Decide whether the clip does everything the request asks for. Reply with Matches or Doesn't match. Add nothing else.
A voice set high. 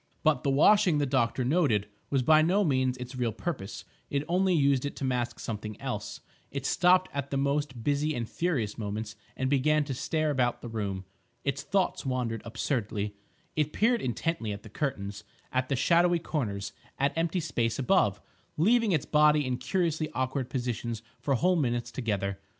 Doesn't match